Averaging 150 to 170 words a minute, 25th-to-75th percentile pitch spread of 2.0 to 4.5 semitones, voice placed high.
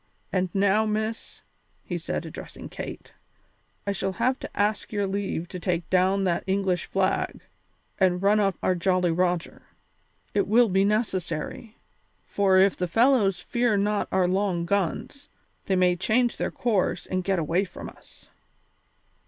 Yes: average, 155 wpm; narrow, 2.4 semitones; high, 195 Hz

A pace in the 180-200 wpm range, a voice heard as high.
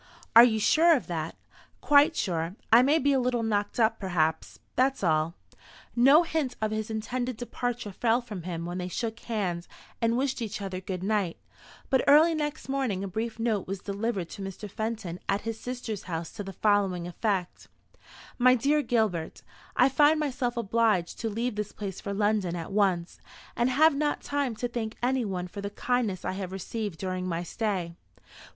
Yes: average, 185 wpm; high, 220 Hz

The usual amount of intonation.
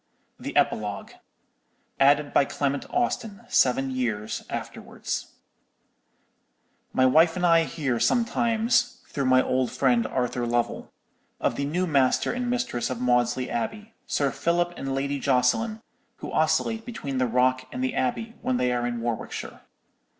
No: wide, 5.9 semitones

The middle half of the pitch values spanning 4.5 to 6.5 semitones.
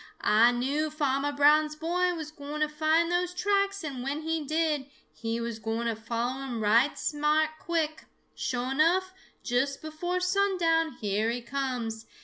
Yes: average, 5.0 semitones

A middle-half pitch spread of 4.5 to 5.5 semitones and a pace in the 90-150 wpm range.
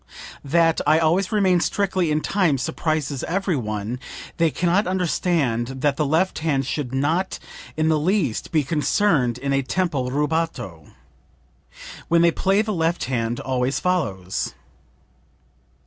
Yes: average, 5.1 semitones; average, 140 wpm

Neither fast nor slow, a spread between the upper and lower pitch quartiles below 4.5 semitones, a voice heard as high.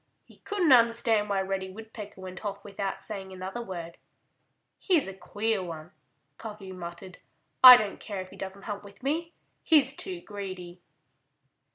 Yes: average, 155 wpm; average, 3.4 semitones; high, 200 Hz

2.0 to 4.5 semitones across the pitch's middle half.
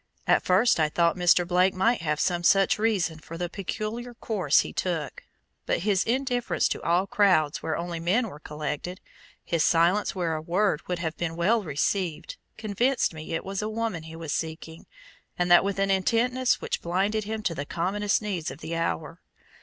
Yes: average, 4.1 semitones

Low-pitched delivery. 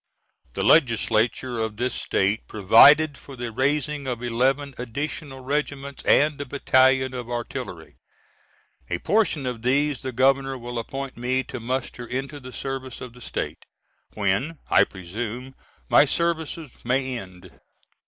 Yes: low, 130 Hz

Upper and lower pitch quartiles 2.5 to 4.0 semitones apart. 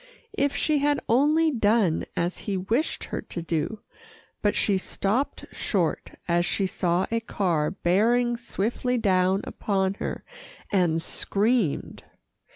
No: average, 4.8 semitones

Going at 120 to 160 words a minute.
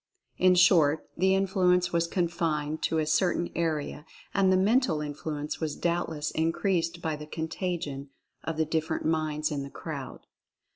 Yes: average, 150 wpm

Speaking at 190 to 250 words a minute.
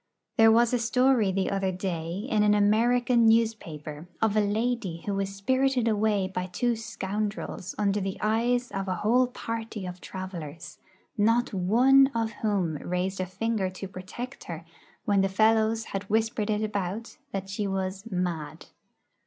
No: average, 160 wpm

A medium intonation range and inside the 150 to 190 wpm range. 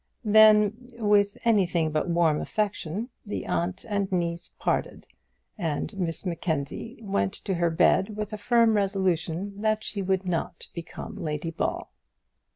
No: average, 3.9 semitones; average, 140 wpm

